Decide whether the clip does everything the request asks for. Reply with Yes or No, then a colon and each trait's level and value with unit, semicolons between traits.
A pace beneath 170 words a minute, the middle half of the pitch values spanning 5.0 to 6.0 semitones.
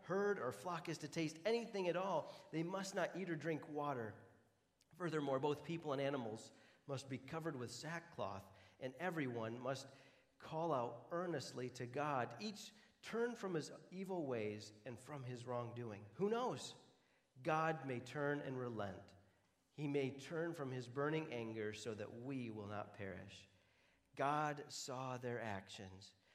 Yes: average, 155 wpm; wide, 5.6 semitones